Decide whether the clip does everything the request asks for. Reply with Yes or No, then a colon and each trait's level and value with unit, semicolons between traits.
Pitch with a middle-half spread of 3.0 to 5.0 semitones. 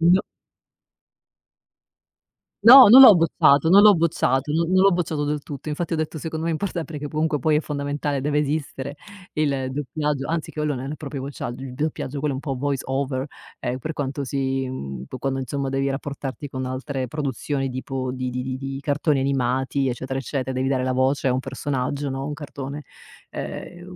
No: narrow, 2.4 semitones